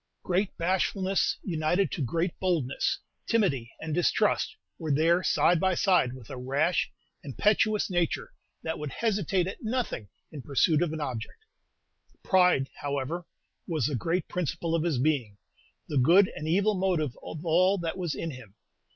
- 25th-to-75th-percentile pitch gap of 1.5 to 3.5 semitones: No, average, 4.5 semitones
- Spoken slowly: No, average, 155 wpm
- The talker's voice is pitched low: No, medium, 165 Hz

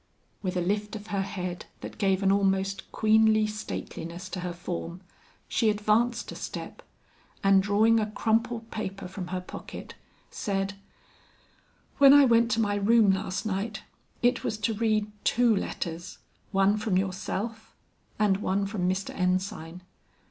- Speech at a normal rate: Yes, average, 150 wpm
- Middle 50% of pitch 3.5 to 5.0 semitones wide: No, narrow, 2.6 semitones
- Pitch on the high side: Yes, high, 200 Hz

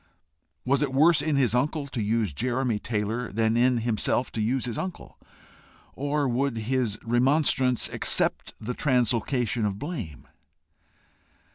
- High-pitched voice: No, low, 125 Hz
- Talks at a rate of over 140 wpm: No, slow, 135 wpm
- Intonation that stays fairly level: No, average, 3.4 semitones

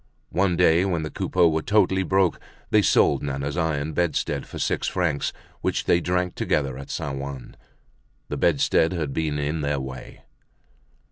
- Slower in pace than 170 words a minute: Yes, average, 160 wpm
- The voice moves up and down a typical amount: Yes, average, 3.9 semitones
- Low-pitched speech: Yes, very low, 80 Hz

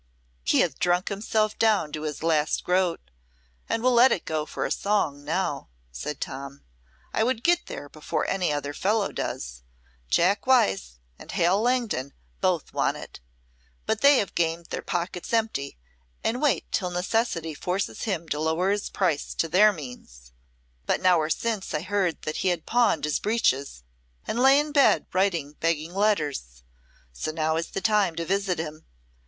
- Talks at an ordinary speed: Yes, average, 170 wpm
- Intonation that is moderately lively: No, wide, 5.7 semitones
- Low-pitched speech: No, medium, 175 Hz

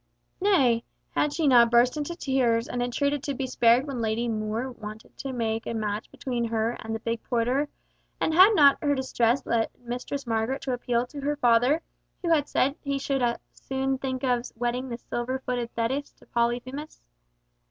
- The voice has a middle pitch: No, very high, 250 Hz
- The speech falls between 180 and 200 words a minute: Yes, average, 185 wpm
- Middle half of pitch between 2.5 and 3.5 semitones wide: Yes, average, 2.9 semitones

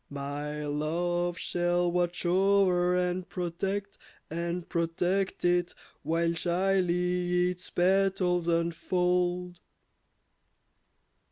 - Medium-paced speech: No, slow, 80 wpm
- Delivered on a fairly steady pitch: Yes, narrow, 1.1 semitones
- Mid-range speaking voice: Yes, medium, 175 Hz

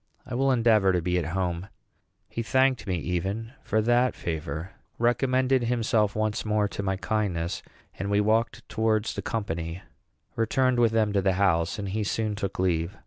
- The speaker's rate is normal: Yes, average, 175 wpm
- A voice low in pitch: Yes, low, 105 Hz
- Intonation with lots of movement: No, average, 3.7 semitones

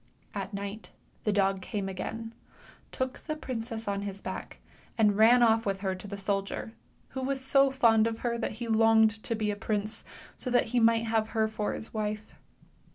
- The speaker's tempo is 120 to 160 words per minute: No, average, 195 wpm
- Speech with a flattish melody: Yes, narrow, 2.1 semitones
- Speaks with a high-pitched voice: Yes, high, 220 Hz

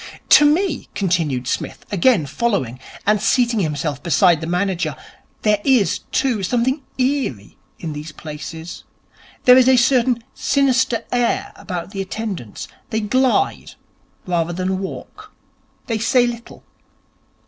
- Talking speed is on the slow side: Yes, slow, 125 wpm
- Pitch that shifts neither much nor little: No, wide, 6.8 semitones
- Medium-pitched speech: No, high, 210 Hz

